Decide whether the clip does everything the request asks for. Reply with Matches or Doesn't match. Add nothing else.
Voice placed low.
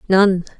Doesn't match